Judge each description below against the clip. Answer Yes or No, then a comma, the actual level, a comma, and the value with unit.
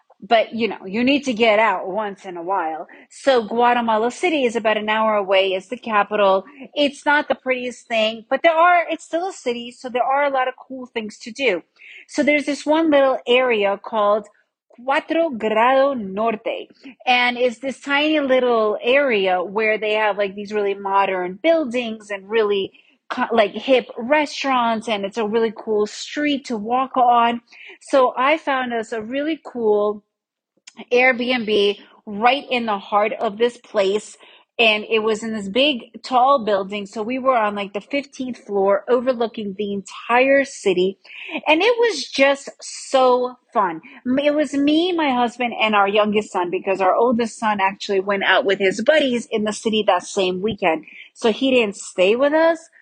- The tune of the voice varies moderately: Yes, average, 4.3 semitones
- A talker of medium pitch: No, high, 235 Hz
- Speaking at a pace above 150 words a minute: Yes, average, 175 wpm